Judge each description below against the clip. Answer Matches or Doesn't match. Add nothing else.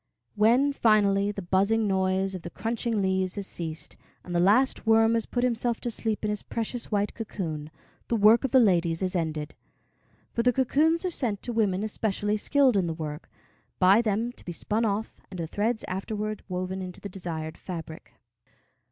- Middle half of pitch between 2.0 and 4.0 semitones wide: Matches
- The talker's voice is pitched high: Matches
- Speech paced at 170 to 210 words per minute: Matches